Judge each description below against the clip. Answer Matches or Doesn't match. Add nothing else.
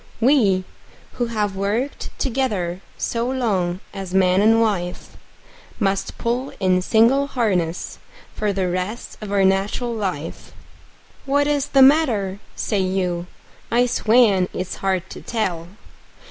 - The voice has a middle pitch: Doesn't match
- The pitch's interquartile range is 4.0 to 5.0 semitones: Matches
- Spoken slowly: Matches